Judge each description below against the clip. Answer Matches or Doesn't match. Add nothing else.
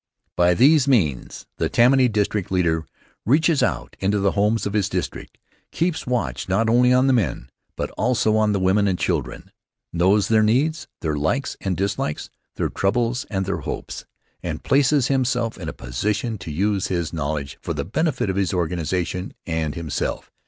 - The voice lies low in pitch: Matches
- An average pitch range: Doesn't match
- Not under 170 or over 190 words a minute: Matches